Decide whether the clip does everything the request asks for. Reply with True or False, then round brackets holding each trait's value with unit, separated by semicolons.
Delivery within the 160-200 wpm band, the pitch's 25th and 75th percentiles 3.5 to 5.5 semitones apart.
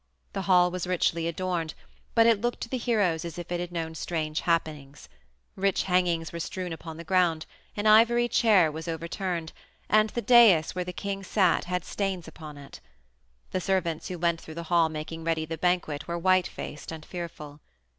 False (190 wpm; 2.5 semitones)